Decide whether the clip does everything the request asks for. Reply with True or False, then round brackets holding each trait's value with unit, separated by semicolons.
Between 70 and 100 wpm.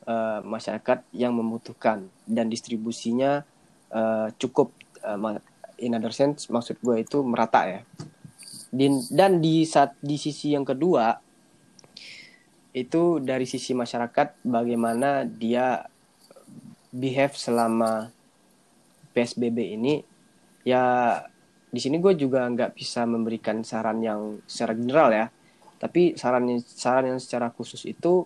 False (115 wpm)